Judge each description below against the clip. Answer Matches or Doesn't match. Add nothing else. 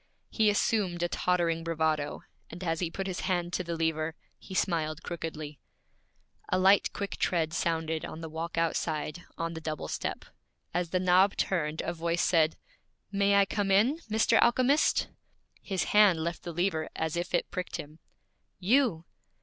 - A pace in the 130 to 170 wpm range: Matches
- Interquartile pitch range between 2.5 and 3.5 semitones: Matches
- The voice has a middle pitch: Matches